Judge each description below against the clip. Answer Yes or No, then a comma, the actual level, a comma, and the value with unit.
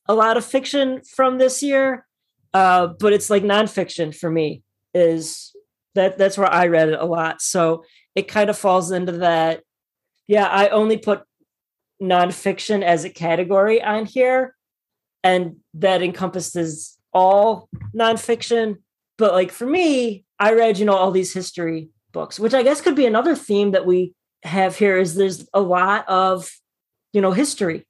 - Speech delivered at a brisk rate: No, average, 165 wpm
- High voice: Yes, high, 195 Hz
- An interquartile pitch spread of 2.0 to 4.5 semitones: Yes, average, 3.7 semitones